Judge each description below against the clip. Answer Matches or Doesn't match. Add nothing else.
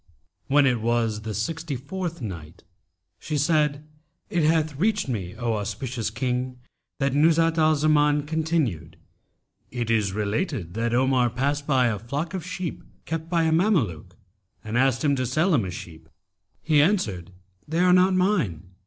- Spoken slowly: Doesn't match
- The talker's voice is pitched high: Doesn't match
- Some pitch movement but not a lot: Doesn't match